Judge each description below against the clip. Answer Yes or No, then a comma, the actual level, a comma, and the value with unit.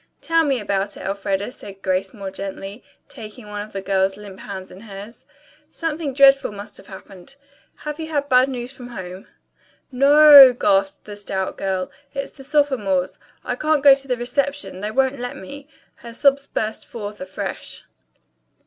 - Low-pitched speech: No, high, 235 Hz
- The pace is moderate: Yes, average, 175 wpm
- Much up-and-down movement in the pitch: Yes, wide, 5.9 semitones